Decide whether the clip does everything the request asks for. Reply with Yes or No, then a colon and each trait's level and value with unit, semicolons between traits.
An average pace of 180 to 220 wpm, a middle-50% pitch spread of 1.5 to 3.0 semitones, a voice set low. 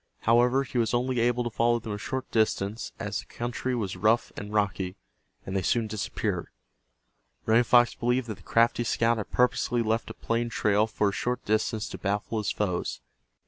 Yes: average, 190 wpm; narrow, 2.4 semitones; low, 115 Hz